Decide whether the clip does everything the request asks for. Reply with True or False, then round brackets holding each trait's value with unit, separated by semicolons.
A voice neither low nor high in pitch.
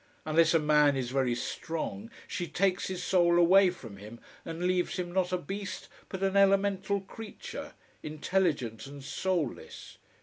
True (175 Hz)